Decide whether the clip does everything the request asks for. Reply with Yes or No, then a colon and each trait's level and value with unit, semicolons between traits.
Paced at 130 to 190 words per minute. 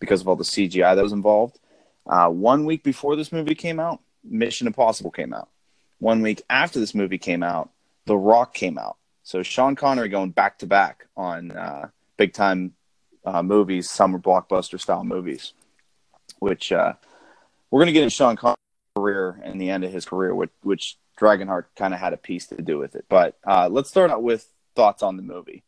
No: average, 200 wpm